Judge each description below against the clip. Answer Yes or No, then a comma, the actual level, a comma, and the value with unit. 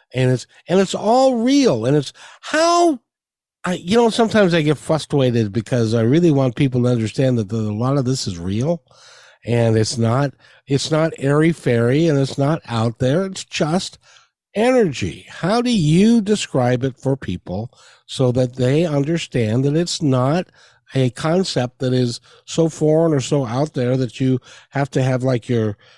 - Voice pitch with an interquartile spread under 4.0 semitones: No, average, 5.2 semitones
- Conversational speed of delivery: Yes, average, 175 wpm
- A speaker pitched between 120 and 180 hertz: Yes, medium, 140 Hz